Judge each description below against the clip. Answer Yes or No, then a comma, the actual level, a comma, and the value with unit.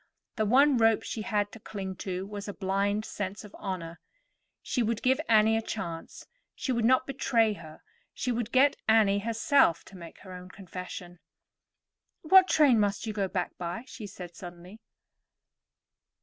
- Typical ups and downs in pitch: Yes, average, 3.6 semitones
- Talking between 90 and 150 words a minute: No, average, 165 wpm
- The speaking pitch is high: Yes, high, 210 Hz